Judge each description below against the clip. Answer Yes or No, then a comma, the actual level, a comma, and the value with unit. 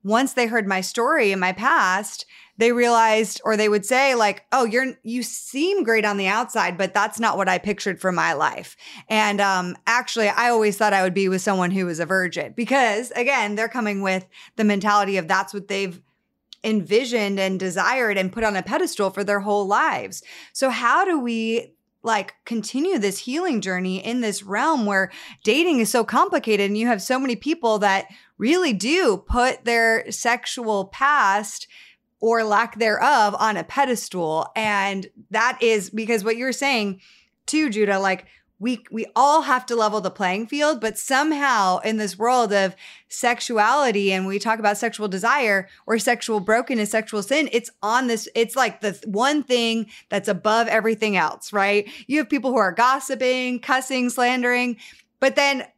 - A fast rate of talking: No, average, 180 wpm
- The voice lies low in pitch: No, high, 225 Hz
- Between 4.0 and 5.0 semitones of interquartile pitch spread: No, average, 3.5 semitones